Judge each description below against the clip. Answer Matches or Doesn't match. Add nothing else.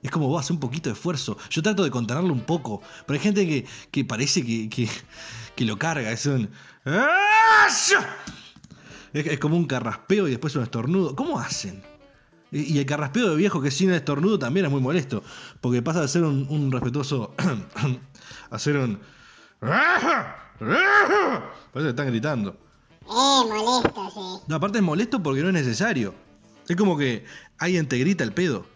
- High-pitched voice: Doesn't match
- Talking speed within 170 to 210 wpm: Matches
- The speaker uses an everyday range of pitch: Doesn't match